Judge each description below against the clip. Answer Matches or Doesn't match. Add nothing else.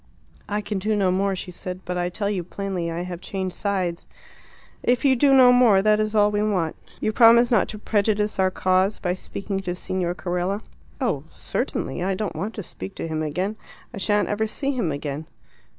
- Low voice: Doesn't match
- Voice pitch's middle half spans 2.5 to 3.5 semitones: Matches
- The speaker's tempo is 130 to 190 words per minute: Doesn't match